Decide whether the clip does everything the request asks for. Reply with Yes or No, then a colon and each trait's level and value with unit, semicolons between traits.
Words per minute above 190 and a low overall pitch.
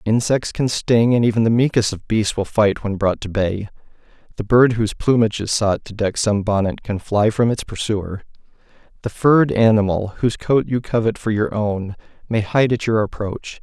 Yes: average, 200 wpm; low, 110 Hz